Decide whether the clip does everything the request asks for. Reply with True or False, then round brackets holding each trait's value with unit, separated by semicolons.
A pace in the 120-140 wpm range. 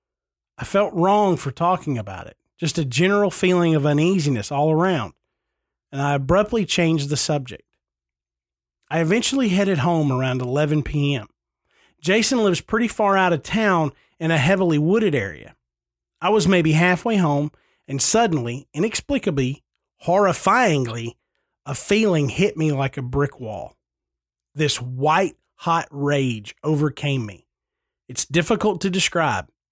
True (135 wpm)